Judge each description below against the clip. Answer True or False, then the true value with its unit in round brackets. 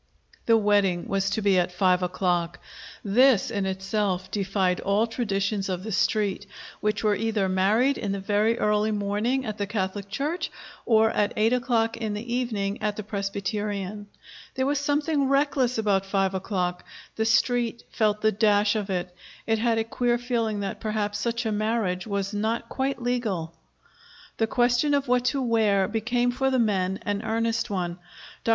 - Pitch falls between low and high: False (215 Hz)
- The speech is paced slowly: False (170 wpm)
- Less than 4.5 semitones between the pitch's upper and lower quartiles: True (3.0 semitones)